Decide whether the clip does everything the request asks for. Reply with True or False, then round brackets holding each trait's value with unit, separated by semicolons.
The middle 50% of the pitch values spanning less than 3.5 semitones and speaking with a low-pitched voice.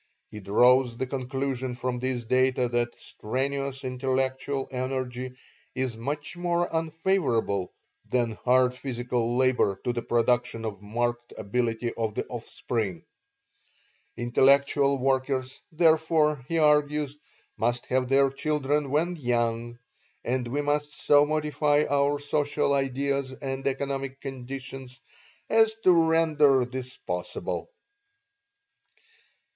True (2.9 semitones; 130 Hz)